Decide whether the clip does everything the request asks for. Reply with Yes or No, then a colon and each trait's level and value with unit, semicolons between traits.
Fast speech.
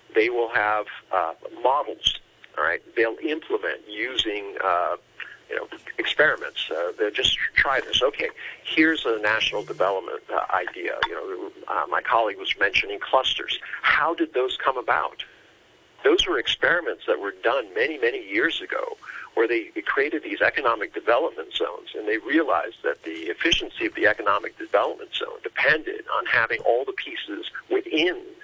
No: average, 160 wpm